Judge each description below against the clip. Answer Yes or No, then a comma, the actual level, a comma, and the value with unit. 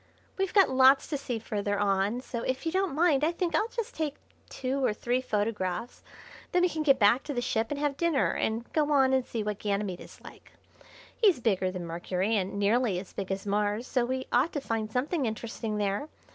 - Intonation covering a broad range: Yes, wide, 5.8 semitones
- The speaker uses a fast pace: Yes, fast, 215 wpm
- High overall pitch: Yes, high, 245 Hz